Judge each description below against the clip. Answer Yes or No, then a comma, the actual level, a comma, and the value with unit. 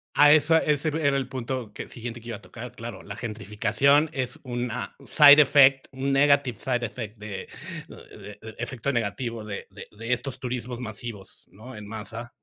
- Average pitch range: Yes, average, 3.7 semitones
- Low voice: Yes, low, 120 Hz